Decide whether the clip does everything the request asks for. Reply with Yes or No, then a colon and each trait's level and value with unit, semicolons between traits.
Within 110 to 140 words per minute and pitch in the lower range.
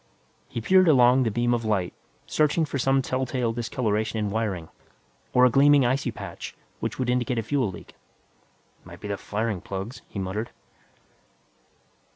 No: average, 160 wpm; low, 120 Hz